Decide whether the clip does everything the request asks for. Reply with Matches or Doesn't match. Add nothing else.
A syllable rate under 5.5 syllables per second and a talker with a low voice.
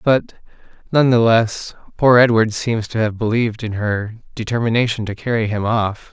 Matches